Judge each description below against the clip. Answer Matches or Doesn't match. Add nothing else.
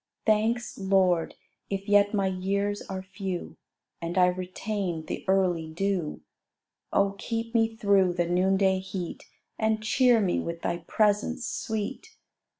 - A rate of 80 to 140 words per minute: Matches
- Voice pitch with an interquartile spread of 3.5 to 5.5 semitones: Doesn't match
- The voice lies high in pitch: Matches